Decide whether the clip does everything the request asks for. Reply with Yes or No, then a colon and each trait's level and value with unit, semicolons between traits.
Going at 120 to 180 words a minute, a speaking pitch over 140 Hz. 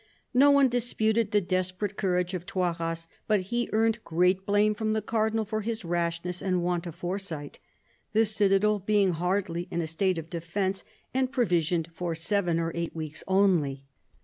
Yes: average, 170 wpm; medium, 185 Hz